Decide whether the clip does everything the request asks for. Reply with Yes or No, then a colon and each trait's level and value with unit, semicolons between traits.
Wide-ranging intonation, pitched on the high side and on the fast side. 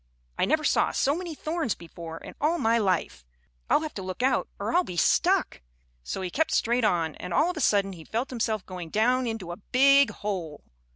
Yes: wide, 7.5 semitones; high, 225 Hz; fast, 215 wpm